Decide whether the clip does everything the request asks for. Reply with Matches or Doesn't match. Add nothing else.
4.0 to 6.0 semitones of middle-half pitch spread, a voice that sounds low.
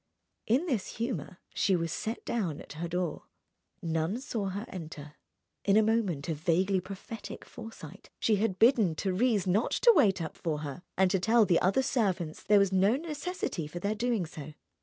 Doesn't match